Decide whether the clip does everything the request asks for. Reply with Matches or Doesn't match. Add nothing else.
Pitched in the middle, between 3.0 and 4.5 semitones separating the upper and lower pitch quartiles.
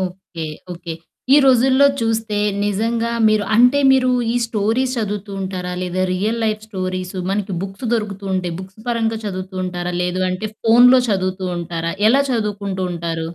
Doesn't match